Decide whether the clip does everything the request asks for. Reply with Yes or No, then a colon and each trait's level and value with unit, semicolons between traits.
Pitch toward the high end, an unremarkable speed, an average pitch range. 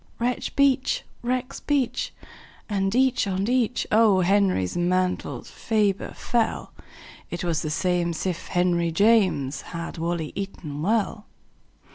No: high, 195 Hz; slow, 100 wpm; average, 4.9 semitones